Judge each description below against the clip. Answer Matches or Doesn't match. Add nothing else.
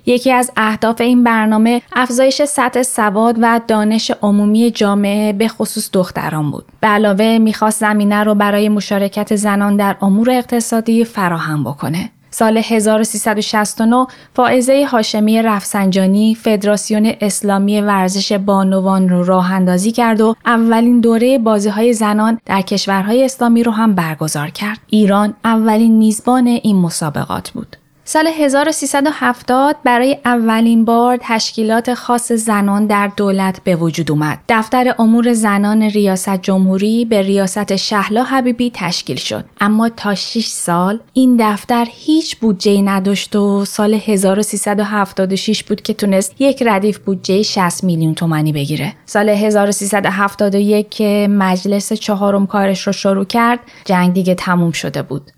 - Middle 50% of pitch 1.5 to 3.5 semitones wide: Matches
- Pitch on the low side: Doesn't match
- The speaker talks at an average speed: Matches